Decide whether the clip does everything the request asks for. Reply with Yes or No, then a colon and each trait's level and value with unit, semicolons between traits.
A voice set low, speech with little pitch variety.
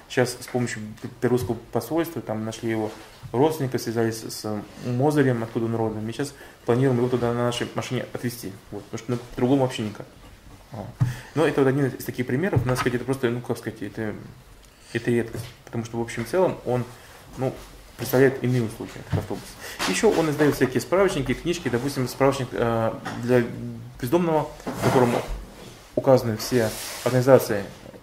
Yes: low, 120 Hz; narrow, 2.2 semitones